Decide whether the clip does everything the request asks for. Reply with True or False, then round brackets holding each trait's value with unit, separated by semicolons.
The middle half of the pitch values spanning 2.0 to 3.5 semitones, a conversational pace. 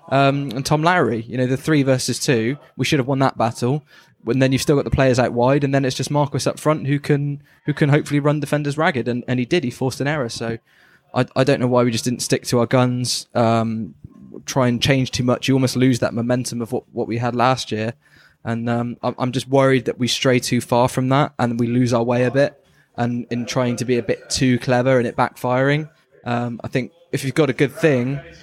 False (2.5 semitones; 250 wpm)